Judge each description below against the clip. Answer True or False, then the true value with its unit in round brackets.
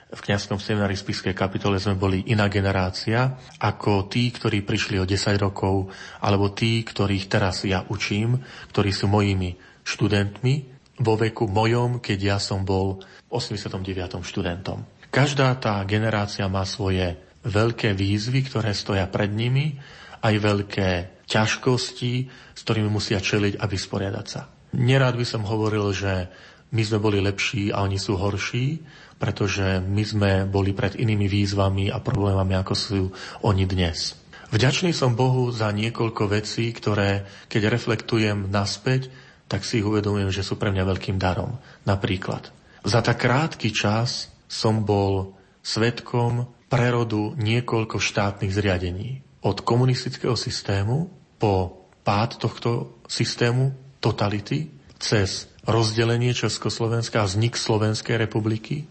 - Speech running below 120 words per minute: False (130 wpm)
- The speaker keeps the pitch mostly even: False (3.1 semitones)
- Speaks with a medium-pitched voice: False (105 Hz)